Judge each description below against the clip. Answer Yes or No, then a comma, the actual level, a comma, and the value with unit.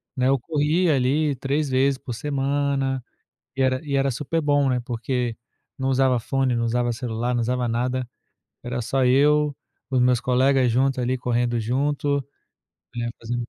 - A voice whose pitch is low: Yes, low, 130 Hz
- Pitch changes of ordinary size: No, narrow, 2.3 semitones